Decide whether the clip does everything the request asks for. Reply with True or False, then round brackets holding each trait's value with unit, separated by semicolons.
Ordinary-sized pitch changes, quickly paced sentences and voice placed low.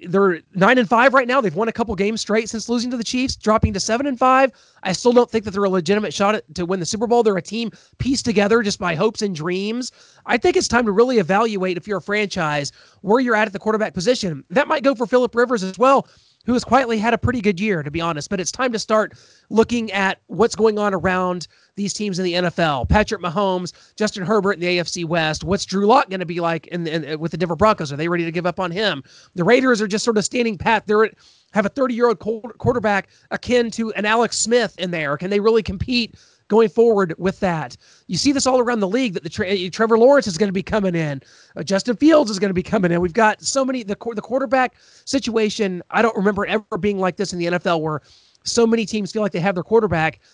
False (4.1 semitones; 250 wpm; 210 Hz)